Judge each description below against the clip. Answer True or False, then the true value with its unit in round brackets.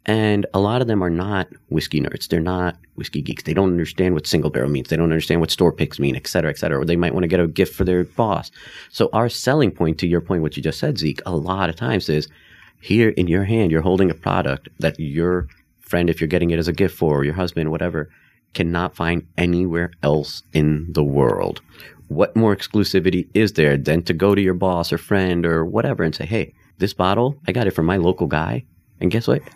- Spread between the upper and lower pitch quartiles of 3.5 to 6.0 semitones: False (2.9 semitones)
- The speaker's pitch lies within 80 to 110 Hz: True (85 Hz)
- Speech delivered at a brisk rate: True (240 wpm)